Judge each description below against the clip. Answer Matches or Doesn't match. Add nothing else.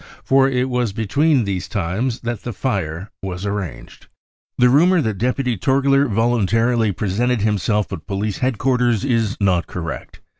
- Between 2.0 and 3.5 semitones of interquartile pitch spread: Doesn't match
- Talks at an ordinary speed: Matches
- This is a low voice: Matches